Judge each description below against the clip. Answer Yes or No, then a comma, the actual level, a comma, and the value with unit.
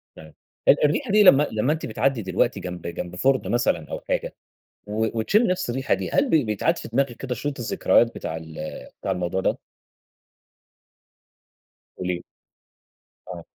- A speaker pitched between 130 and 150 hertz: No, low, 115 Hz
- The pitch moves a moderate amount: No, wide, 7.5 semitones